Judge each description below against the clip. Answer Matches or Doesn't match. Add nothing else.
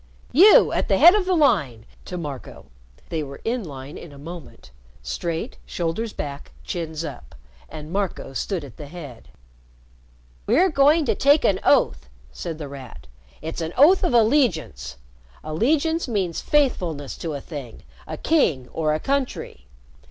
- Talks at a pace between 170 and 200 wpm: Doesn't match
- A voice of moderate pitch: Matches